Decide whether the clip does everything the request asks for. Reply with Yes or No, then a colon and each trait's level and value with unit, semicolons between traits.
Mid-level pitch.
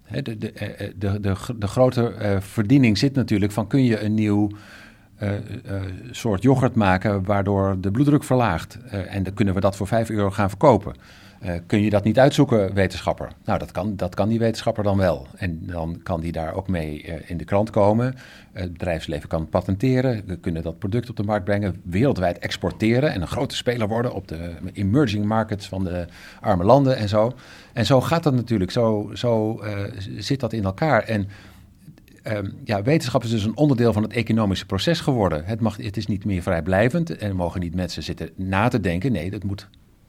No: low, 105 Hz